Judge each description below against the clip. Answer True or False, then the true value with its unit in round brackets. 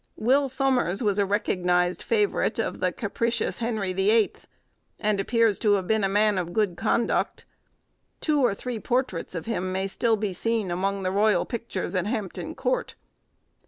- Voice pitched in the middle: False (210 Hz)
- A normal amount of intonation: True (3.5 semitones)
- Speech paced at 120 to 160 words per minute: False (170 wpm)